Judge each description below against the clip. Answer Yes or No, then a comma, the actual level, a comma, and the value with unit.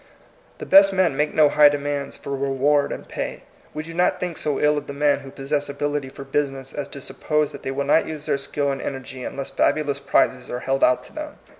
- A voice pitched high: No, medium, 140 Hz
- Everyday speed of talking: No, fast, 240 wpm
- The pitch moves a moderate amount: No, narrow, 1.6 semitones